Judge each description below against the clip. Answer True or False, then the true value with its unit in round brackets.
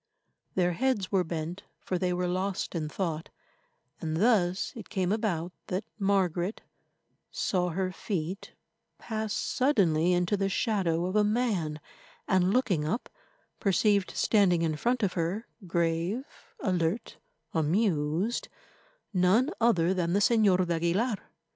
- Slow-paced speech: True (130 wpm)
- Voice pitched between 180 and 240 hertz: True (185 Hz)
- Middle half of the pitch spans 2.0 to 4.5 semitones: True (3.5 semitones)